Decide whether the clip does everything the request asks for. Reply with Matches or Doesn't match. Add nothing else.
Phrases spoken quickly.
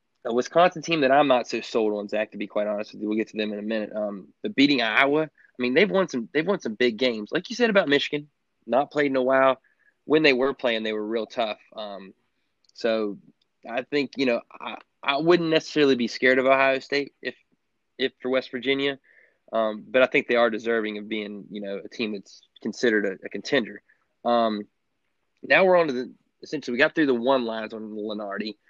Matches